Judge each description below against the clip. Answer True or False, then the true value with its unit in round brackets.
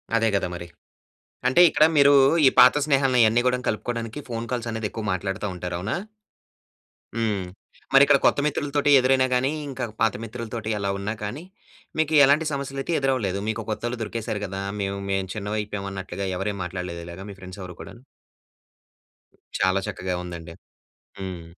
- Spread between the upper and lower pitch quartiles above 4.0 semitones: True (4.7 semitones)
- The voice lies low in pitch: True (110 Hz)